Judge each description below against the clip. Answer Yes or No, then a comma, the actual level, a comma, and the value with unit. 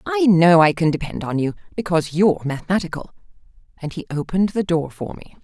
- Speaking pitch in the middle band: Yes, medium, 175 Hz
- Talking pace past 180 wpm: Yes, average, 190 wpm